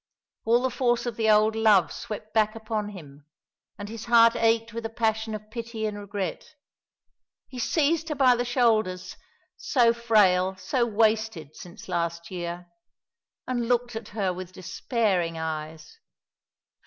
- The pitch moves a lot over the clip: No, average, 4.0 semitones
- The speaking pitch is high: Yes, high, 220 Hz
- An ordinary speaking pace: Yes, average, 150 wpm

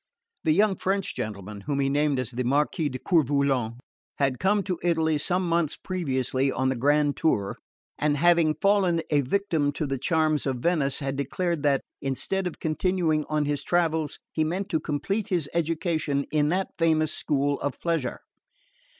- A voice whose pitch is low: No, medium, 155 Hz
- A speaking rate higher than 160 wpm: Yes, average, 175 wpm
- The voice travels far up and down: No, average, 3.6 semitones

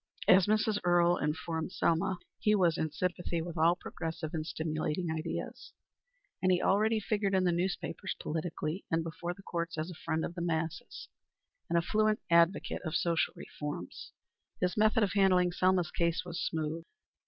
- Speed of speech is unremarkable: Yes, average, 165 wpm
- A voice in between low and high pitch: Yes, medium, 175 Hz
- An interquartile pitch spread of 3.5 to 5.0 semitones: No, narrow, 2.6 semitones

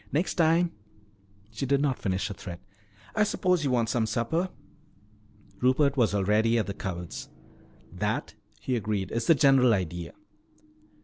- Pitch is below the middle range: Yes, low, 115 Hz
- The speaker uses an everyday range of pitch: No, wide, 5.9 semitones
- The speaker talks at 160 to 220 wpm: No, average, 150 wpm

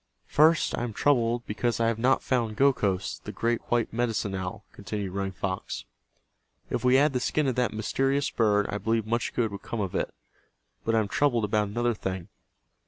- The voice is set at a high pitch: No, low, 115 Hz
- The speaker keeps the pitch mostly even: No, average, 3.2 semitones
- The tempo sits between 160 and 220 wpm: Yes, average, 195 wpm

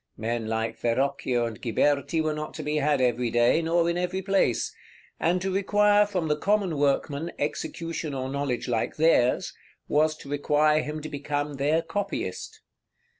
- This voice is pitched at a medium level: Yes, medium, 150 Hz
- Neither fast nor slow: Yes, average, 165 wpm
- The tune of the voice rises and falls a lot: No, average, 3.8 semitones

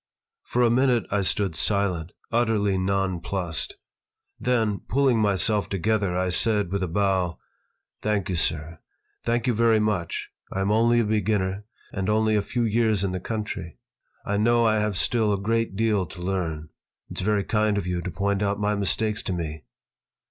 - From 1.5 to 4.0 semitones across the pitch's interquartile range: Yes, average, 2.9 semitones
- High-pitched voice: No, low, 100 Hz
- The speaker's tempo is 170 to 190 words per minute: Yes, average, 175 wpm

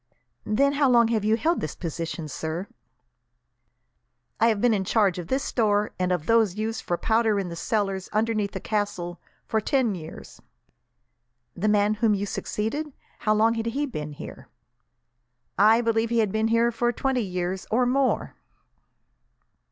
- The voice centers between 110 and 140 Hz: No, high, 215 Hz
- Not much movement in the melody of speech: No, average, 3.3 semitones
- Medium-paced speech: Yes, average, 165 wpm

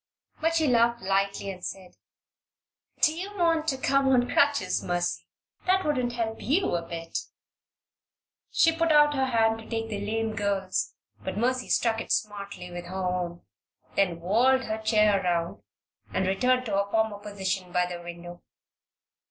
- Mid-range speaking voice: No, high, 215 Hz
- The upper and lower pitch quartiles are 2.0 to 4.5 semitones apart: No, wide, 5.5 semitones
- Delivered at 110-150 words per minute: No, average, 165 wpm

